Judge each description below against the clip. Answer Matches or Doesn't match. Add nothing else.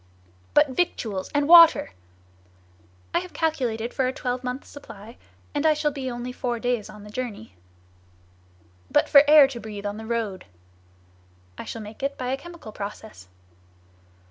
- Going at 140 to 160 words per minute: Matches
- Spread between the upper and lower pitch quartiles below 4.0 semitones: Doesn't match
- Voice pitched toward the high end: Matches